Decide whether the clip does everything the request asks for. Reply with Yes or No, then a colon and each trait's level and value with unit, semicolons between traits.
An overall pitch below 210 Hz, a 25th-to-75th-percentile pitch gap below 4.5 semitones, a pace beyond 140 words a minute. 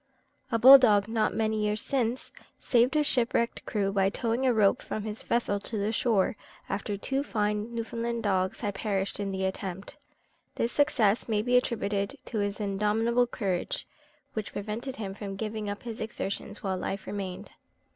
No: high, 215 Hz; average, 2.8 semitones; average, 170 wpm